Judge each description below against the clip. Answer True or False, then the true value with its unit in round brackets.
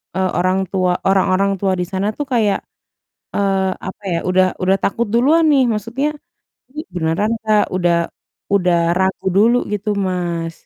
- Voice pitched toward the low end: False (195 Hz)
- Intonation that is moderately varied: True (3.0 semitones)